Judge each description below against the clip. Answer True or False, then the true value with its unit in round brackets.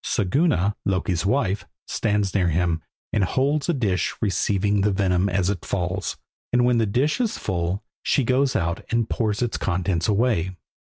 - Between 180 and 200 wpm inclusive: False (165 wpm)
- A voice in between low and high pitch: False (100 Hz)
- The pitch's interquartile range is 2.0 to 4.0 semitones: False (4.4 semitones)